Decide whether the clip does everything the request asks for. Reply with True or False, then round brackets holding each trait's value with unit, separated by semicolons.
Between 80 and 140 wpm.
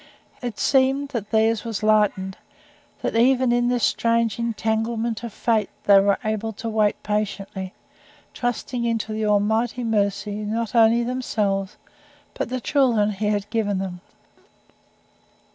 True (135 wpm)